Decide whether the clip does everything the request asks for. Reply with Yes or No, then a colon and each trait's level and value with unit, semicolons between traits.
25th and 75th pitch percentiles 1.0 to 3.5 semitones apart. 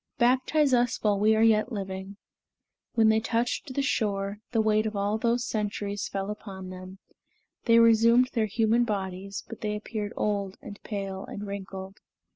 Yes: narrow, 2.6 semitones